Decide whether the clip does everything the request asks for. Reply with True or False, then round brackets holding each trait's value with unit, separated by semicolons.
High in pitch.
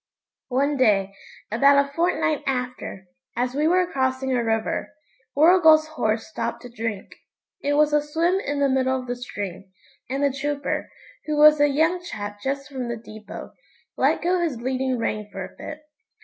True (270 Hz)